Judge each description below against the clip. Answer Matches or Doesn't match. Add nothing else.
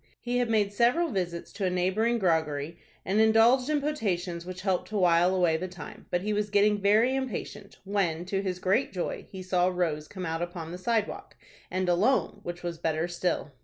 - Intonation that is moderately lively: Matches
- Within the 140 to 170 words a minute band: Doesn't match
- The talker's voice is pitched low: Doesn't match